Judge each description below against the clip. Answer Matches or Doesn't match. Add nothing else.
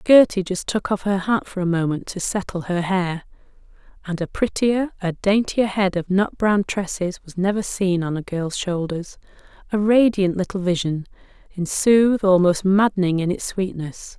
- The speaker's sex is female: Matches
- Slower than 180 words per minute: Matches